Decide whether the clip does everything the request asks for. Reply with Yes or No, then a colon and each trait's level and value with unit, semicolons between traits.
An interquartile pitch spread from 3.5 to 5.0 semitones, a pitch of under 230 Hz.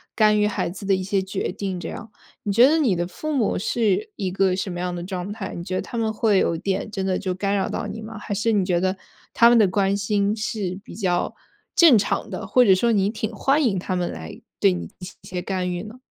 No: average, 2.8 semitones; high, 200 Hz